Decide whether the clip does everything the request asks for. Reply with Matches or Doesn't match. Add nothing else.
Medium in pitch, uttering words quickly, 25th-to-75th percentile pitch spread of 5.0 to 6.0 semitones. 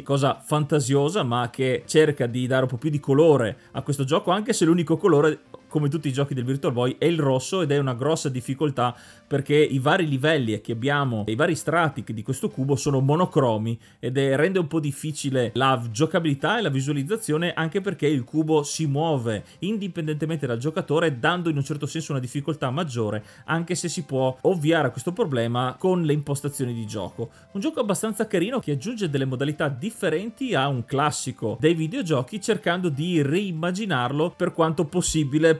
Doesn't match